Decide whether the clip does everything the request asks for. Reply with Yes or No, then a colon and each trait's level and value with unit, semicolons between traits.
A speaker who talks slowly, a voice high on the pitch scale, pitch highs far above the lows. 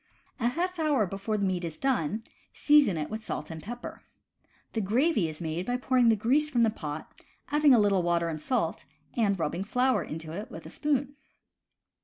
No: average, 195 wpm; high, 220 Hz; wide, 7.1 semitones